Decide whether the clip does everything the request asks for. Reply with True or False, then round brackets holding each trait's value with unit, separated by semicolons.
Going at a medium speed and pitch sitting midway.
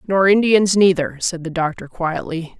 True (160 wpm; 180 Hz)